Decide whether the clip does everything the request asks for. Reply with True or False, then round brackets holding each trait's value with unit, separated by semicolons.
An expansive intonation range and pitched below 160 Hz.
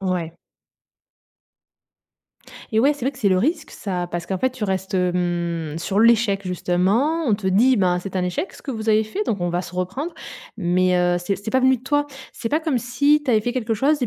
False (6.1 semitones; 205 Hz)